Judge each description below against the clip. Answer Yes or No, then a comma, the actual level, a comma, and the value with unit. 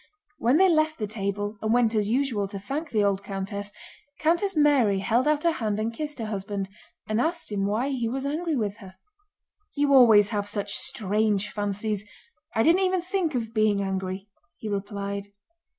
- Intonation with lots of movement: Yes, wide, 5.7 semitones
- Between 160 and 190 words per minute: Yes, average, 180 wpm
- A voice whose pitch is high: Yes, high, 220 Hz